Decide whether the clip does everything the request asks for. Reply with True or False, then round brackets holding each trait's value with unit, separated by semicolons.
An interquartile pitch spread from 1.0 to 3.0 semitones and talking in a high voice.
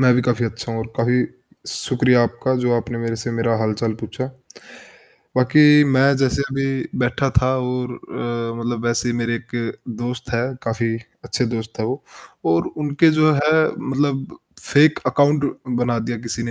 False (2.4 semitones; 125 Hz)